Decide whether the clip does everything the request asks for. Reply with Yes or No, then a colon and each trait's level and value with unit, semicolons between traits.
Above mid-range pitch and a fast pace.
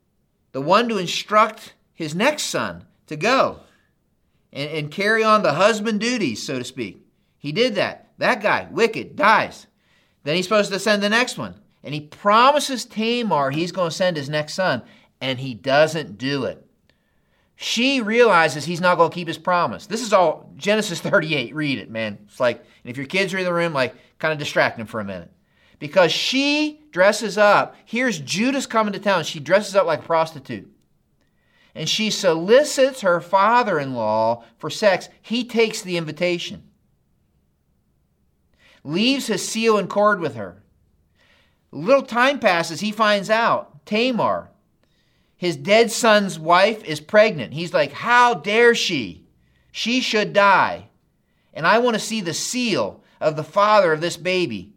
No: high, 195 Hz; average, 170 wpm